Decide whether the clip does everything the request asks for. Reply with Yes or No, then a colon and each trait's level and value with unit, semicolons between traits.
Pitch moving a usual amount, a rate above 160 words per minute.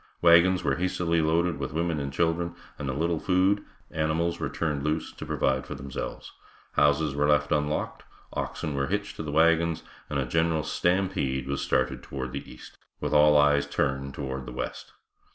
Yes: average, 3.4 semitones; average, 180 wpm